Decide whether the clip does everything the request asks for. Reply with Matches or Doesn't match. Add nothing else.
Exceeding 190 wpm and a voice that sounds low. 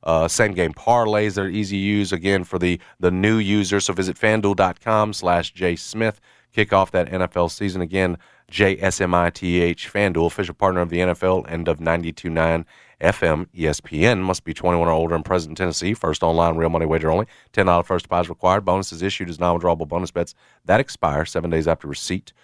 Matches